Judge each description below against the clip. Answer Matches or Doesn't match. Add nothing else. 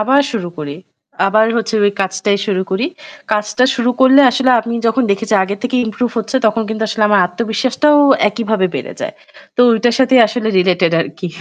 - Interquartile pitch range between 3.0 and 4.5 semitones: Matches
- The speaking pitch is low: Doesn't match